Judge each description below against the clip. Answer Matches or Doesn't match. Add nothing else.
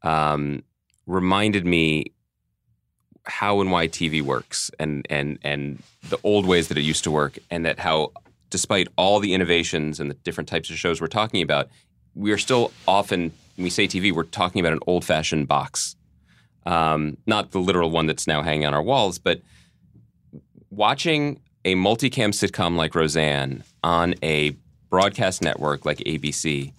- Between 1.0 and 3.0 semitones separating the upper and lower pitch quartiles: Doesn't match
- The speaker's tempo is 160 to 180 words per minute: Matches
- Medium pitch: Doesn't match